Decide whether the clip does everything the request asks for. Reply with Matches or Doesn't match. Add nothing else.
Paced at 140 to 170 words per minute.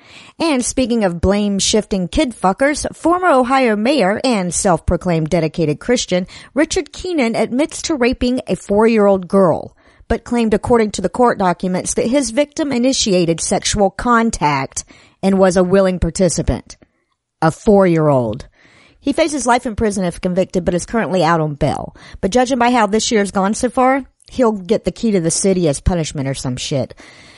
Doesn't match